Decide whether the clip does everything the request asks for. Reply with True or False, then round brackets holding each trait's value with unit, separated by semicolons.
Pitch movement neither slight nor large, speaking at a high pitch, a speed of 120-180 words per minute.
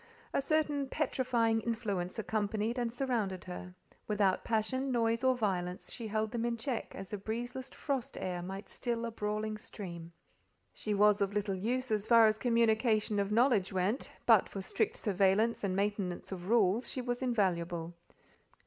True (3.4 semitones; 215 Hz; 165 wpm)